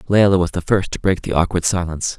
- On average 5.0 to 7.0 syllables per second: Yes, 6.4 syllables/s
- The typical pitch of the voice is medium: No, very low, 90 Hz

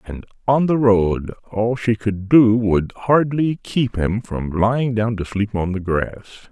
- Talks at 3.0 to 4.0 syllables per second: Yes, 3.7 syllables/s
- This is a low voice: Yes, low, 110 Hz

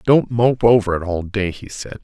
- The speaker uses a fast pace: Yes, fast, 235 wpm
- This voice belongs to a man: Yes, male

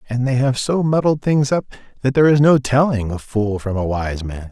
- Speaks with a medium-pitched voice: No, low, 125 Hz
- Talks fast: Yes, fast, 240 wpm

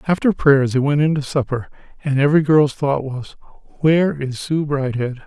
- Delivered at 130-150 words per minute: No, average, 180 wpm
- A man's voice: Yes, male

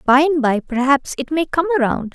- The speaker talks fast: Yes, fast, 225 wpm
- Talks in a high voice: Yes, very high, 285 Hz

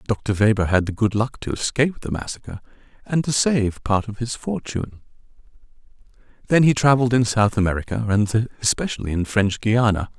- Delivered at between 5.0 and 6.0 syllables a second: Yes, 5.5 syllables/s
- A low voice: Yes, low, 115 Hz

